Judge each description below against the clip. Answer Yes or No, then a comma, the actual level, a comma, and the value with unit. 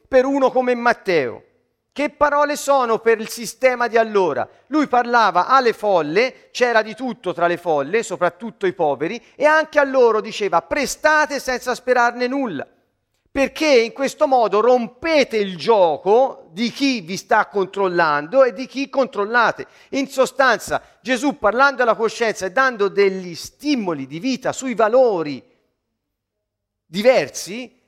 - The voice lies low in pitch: No, high, 245 Hz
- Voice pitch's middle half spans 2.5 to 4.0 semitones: No, average, 5.0 semitones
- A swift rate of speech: No, average, 140 wpm